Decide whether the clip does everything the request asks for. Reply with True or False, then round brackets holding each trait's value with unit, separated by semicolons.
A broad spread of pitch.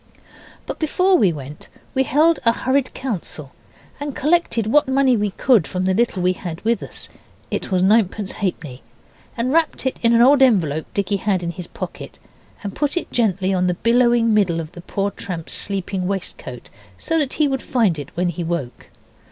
True (6.4 semitones)